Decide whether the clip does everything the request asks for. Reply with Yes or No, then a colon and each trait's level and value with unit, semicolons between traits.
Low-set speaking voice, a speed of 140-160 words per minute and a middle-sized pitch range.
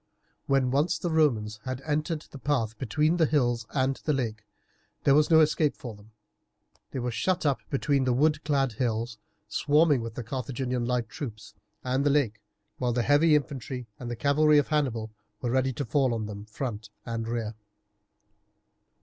No: low, 130 Hz; average, 175 wpm; average, 4.0 semitones